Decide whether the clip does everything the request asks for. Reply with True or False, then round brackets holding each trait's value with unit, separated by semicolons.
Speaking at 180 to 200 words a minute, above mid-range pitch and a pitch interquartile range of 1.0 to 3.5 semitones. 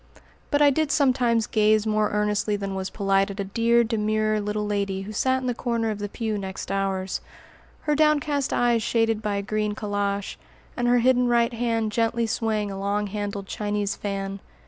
True (190 wpm; 215 Hz; 2.6 semitones)